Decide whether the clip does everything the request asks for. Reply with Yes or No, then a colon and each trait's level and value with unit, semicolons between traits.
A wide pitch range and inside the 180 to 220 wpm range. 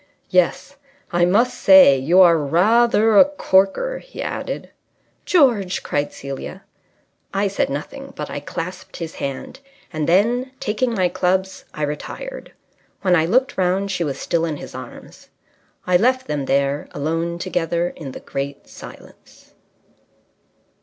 No: wide, 5.8 semitones; average, 140 wpm